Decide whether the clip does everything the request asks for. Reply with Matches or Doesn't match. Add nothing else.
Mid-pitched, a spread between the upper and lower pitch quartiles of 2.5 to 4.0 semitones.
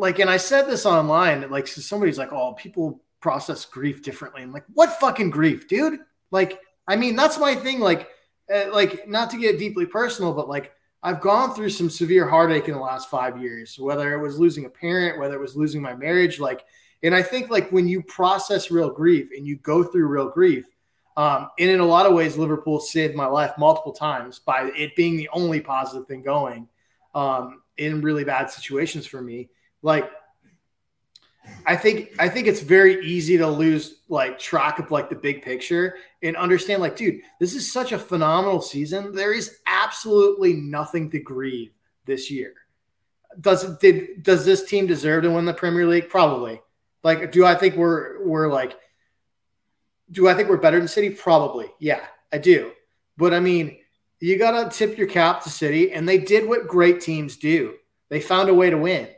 Doesn't match